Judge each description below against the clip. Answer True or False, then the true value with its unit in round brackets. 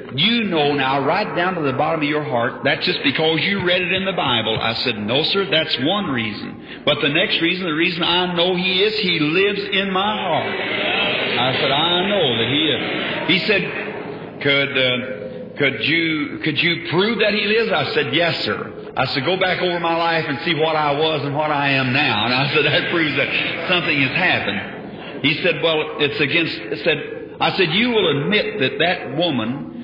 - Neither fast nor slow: False (210 wpm)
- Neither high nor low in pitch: True (160 Hz)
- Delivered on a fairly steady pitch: False (4.2 semitones)